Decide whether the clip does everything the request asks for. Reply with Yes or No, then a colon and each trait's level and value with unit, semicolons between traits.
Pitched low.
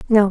No: high, 205 Hz